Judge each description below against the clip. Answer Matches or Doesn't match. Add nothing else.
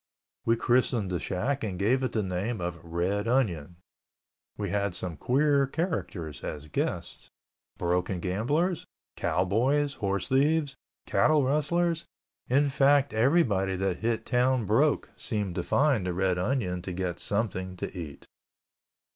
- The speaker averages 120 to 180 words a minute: Matches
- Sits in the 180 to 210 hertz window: Doesn't match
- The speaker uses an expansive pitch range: Matches